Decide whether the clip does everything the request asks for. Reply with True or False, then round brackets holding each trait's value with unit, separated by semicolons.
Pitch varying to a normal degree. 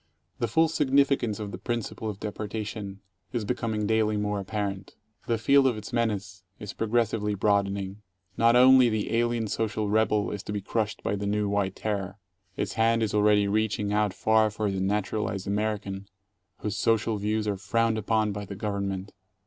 False (1.9 semitones)